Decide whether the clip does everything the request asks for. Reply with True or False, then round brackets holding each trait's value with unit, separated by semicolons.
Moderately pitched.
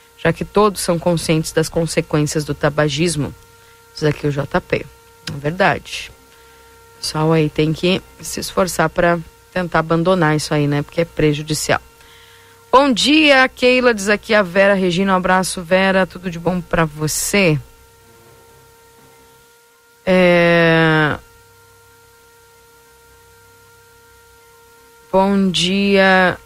True (170 Hz)